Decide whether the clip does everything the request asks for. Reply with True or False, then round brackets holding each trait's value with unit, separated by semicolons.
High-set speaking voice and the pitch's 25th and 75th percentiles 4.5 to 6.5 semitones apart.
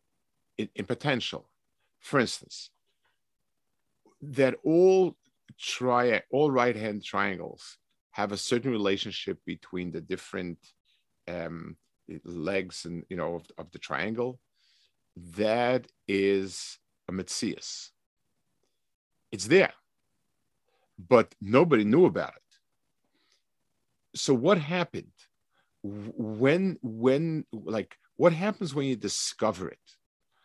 False (110 Hz; 5.6 semitones)